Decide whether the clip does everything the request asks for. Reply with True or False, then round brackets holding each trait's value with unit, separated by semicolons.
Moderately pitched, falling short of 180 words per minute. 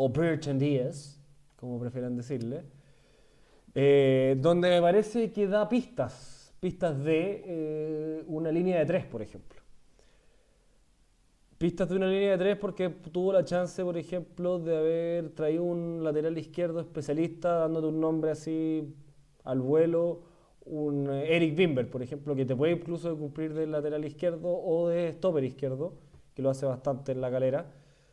True (155 Hz; 155 wpm)